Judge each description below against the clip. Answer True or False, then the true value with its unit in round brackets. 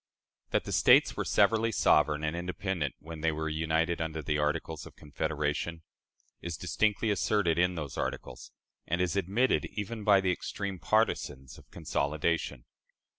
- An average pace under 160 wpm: True (150 wpm)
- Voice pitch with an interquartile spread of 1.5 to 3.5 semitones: False (4.0 semitones)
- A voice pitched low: True (85 Hz)